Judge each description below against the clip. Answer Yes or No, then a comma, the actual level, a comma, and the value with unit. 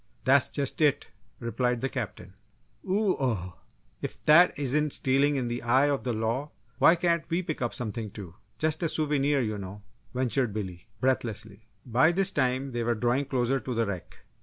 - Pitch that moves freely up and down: No, average, 4.2 semitones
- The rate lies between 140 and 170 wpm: No, average, 180 wpm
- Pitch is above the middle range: No, low, 130 Hz